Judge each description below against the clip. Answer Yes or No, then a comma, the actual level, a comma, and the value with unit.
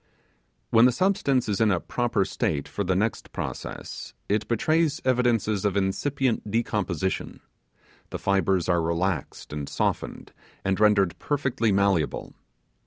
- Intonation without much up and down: No, average, 4.2 semitones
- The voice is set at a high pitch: No, low, 105 Hz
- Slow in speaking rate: Yes, slow, 130 wpm